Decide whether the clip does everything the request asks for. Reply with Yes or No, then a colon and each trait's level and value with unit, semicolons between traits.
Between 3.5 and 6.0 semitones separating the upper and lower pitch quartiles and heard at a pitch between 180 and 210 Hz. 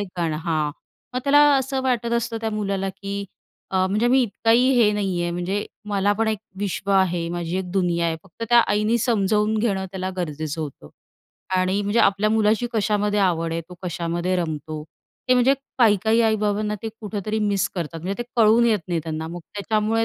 Yes: average, 4.0 semitones; high, 200 Hz